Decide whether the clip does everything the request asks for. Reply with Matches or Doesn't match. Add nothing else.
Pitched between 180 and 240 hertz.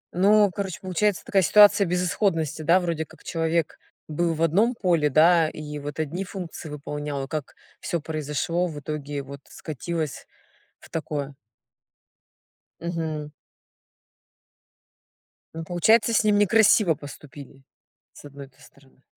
Doesn't match